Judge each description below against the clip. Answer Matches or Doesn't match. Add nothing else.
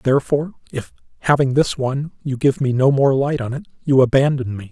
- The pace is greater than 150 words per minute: Matches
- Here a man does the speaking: Matches